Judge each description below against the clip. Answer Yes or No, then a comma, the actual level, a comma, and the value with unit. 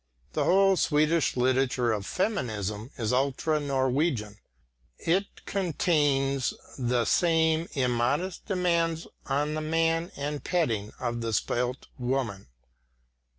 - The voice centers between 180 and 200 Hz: No, medium, 140 Hz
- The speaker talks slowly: Yes, slow, 110 wpm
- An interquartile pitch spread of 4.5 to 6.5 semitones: Yes, average, 5.0 semitones